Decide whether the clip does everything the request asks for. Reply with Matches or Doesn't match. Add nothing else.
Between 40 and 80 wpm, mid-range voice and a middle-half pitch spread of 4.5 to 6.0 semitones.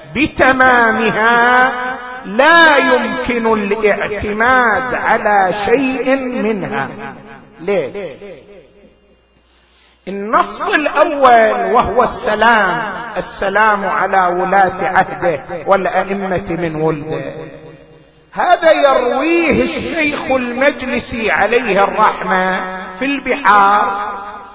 Doesn't match